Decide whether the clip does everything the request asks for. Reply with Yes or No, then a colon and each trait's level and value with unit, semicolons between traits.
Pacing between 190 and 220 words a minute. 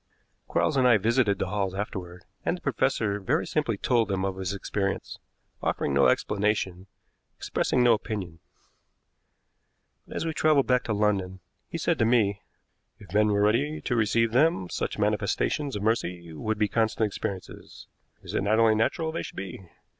No: average, 170 wpm